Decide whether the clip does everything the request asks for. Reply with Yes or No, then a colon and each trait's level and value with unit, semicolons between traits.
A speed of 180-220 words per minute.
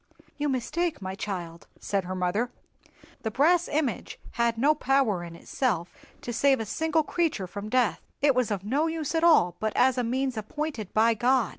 Yes: average, 185 wpm